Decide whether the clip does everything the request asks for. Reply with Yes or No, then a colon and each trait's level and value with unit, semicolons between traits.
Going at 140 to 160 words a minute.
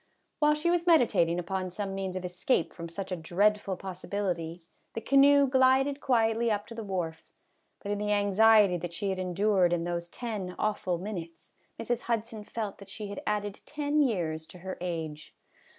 No: average, 180 wpm